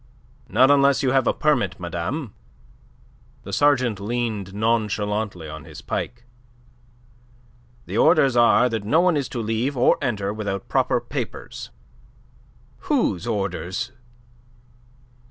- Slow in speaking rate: Yes, slow, 120 wpm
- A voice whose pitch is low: Yes, low, 115 Hz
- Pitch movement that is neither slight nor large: Yes, average, 4.6 semitones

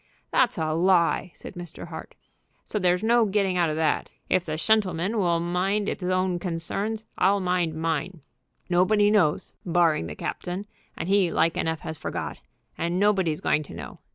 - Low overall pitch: No, medium, 180 Hz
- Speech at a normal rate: Yes, average, 170 wpm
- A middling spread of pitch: Yes, average, 3.1 semitones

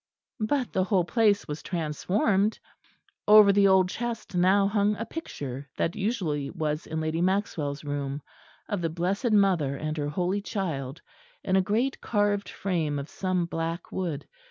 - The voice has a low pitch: No, medium, 185 Hz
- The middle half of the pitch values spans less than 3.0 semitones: No, average, 4.9 semitones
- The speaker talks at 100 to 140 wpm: No, average, 155 wpm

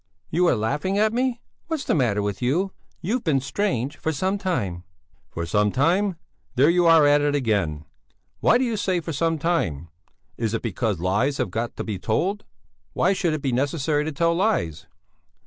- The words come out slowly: No, average, 190 wpm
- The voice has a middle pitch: Yes, medium, 145 Hz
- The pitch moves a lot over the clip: Yes, wide, 8.6 semitones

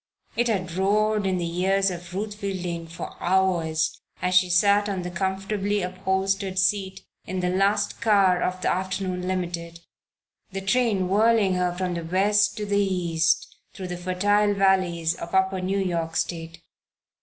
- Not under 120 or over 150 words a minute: No, average, 160 wpm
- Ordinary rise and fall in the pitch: No, narrow, 1.9 semitones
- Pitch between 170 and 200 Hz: Yes, medium, 185 Hz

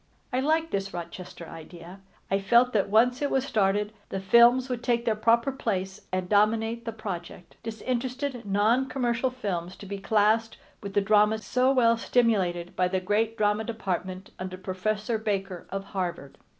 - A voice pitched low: No, high, 210 Hz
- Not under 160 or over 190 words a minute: Yes, average, 165 wpm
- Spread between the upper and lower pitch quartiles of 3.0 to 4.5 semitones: Yes, average, 3.7 semitones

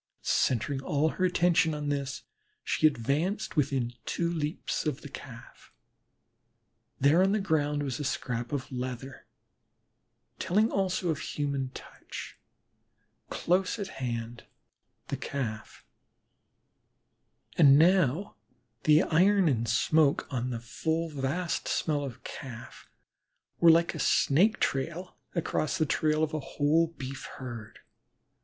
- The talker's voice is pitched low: No, medium, 150 Hz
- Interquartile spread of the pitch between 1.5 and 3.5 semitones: No, average, 4.1 semitones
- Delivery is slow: Yes, slow, 125 wpm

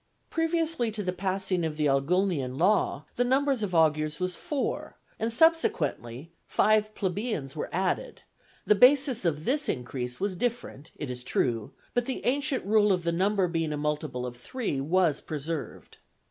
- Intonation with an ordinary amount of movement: No, wide, 7.3 semitones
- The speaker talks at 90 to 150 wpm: No, average, 165 wpm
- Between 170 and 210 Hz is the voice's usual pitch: Yes, medium, 185 Hz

